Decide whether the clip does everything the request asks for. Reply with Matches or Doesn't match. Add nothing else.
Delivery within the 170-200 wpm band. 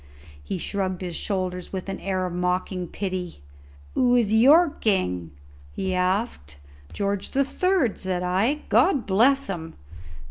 Doesn't match